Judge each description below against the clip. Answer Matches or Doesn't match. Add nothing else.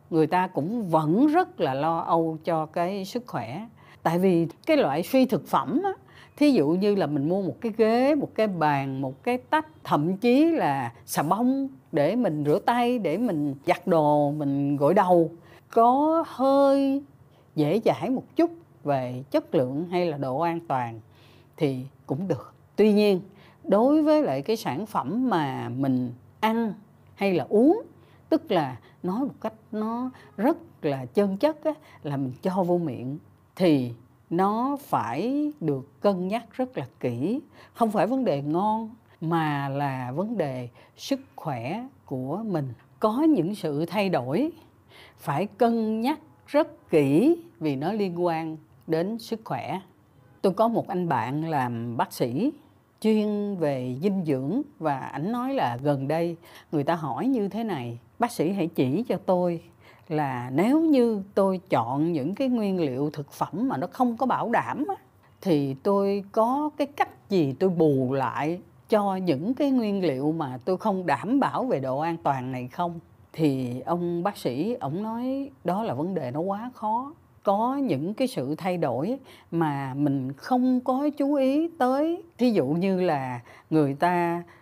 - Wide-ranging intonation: Matches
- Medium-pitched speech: Matches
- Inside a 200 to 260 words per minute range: Doesn't match